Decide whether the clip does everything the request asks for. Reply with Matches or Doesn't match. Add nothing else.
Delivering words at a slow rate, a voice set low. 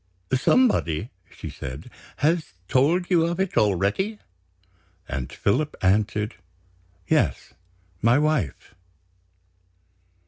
Matches